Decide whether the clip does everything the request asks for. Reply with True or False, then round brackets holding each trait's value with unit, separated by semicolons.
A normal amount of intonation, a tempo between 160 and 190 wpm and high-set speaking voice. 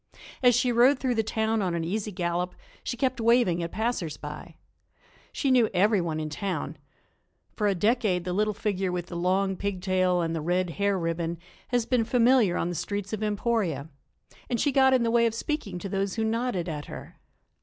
False (4.8 semitones; 200 wpm; 200 Hz)